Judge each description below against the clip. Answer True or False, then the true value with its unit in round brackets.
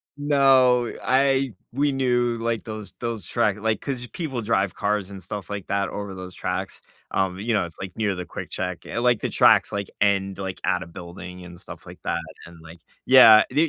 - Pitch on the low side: True (105 Hz)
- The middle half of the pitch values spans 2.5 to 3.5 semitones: False (4.6 semitones)